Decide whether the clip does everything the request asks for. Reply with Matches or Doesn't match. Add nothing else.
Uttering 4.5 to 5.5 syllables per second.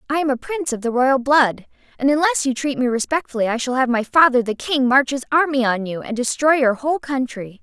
Doesn't match